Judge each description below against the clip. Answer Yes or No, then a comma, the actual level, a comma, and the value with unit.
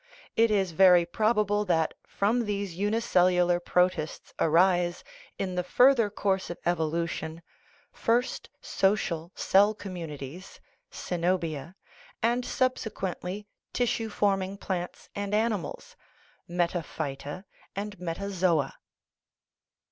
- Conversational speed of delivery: No, slow, 95 wpm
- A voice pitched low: No, medium, 185 Hz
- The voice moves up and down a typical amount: Yes, average, 3.2 semitones